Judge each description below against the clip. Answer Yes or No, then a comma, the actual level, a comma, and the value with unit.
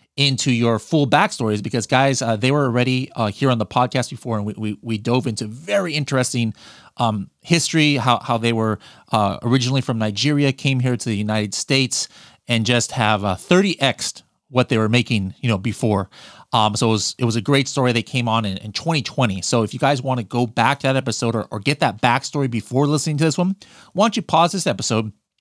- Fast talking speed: Yes, fast, 220 wpm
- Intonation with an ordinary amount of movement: Yes, average, 3.8 semitones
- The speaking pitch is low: Yes, low, 125 Hz